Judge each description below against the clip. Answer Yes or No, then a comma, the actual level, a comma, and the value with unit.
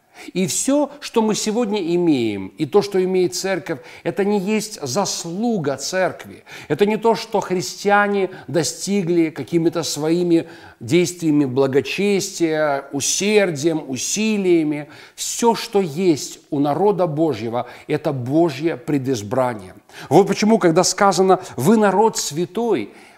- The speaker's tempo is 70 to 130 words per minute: Yes, average, 115 wpm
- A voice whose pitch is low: No, medium, 175 Hz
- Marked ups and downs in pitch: No, average, 5.0 semitones